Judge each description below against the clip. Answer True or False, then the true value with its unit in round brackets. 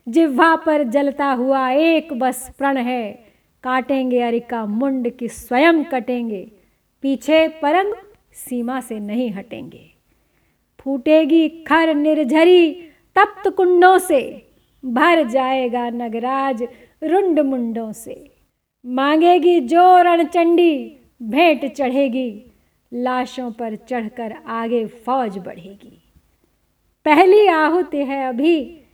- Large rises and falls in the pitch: False (4.7 semitones)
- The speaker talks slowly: True (95 wpm)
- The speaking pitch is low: False (270 Hz)